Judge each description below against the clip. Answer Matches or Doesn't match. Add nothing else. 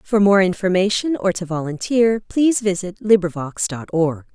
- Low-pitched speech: Doesn't match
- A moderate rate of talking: Matches